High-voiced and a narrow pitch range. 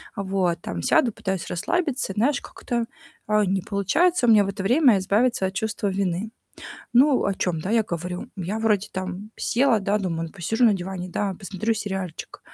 No: high, 200 Hz; average, 3.2 semitones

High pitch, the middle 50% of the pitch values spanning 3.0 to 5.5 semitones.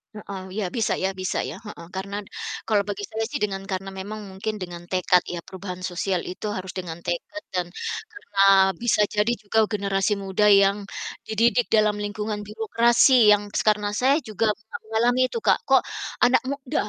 No: high, 205 Hz; narrow, 2.6 semitones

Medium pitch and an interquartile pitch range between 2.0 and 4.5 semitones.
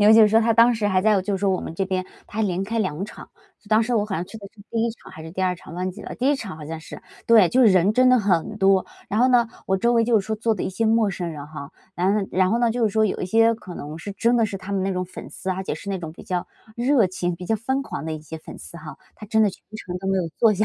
No: high, 200 Hz; average, 3.5 semitones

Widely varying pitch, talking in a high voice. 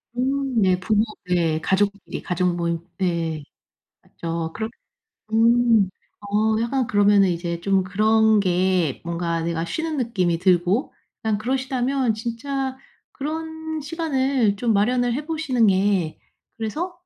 Yes: wide, 6.1 semitones; high, 215 Hz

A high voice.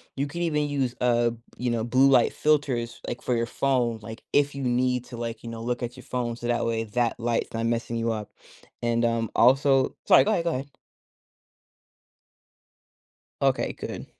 No: low, 120 Hz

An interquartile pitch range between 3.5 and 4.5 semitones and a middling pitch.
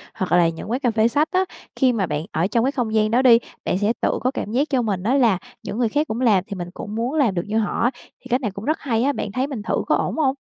No: average, 4.2 semitones; high, 230 Hz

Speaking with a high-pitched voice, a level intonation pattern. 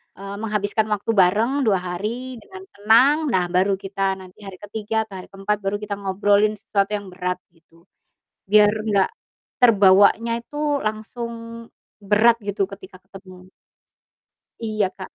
Yes: high, 205 Hz; narrow, 2.2 semitones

